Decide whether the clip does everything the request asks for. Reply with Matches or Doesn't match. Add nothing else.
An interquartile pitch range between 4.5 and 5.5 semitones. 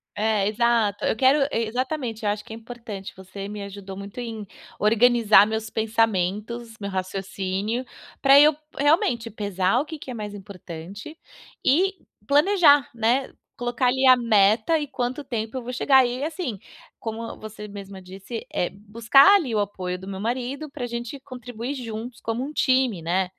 Doesn't match